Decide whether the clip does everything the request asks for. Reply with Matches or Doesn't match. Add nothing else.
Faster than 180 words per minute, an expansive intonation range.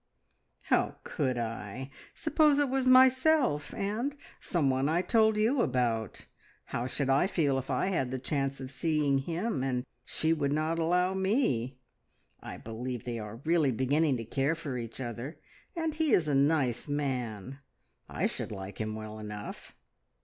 Doesn't match